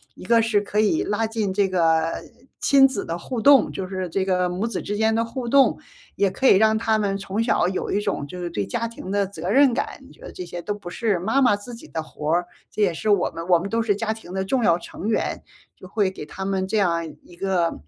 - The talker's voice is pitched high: Yes, high, 200 Hz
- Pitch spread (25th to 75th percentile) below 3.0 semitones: No, average, 3.7 semitones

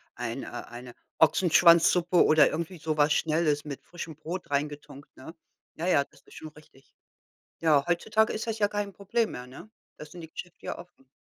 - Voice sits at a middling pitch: Yes, medium, 160 Hz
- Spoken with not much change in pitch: No, average, 3.3 semitones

